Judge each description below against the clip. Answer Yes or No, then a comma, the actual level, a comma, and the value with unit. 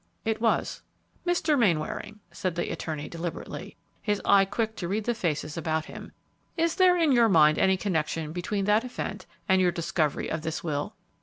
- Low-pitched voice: No, high, 190 Hz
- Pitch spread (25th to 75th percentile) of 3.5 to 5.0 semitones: No, wide, 5.6 semitones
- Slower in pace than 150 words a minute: No, average, 175 wpm